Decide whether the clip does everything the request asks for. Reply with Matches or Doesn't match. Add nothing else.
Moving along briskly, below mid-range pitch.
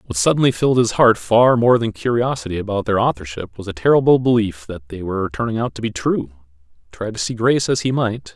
Matches